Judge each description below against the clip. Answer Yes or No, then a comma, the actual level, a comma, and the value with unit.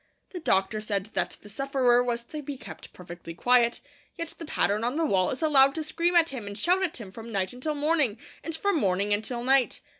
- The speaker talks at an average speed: No, fast, 220 wpm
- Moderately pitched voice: No, high, 245 Hz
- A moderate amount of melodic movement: No, wide, 6.8 semitones